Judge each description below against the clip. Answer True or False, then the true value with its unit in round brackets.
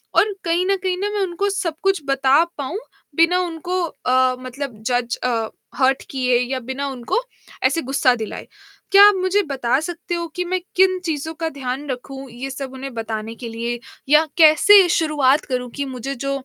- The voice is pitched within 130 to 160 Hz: False (275 Hz)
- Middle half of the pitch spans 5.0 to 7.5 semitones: True (5.3 semitones)